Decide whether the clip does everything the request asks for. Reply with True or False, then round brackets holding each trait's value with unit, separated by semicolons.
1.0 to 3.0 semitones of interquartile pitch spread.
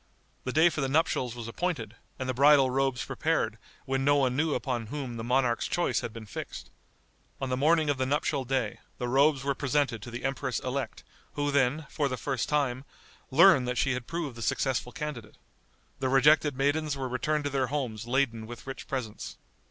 True (2.7 semitones)